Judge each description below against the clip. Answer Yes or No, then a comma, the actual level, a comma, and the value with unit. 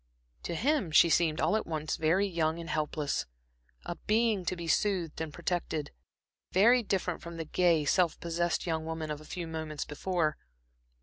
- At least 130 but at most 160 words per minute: No, average, 175 wpm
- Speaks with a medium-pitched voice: Yes, medium, 170 Hz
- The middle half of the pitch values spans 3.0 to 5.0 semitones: No, narrow, 2.6 semitones